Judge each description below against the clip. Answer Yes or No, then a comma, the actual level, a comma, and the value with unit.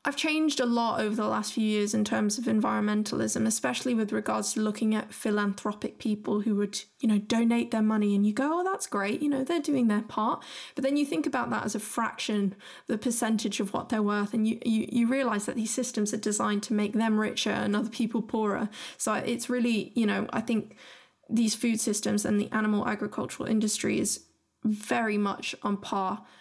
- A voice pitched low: No, high, 220 Hz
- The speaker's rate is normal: No, fast, 210 wpm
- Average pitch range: No, narrow, 2.2 semitones